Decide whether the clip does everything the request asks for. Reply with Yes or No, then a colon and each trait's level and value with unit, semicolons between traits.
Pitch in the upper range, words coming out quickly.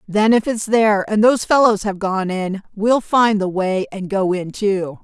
Yes: high, 205 Hz; fast, 215 wpm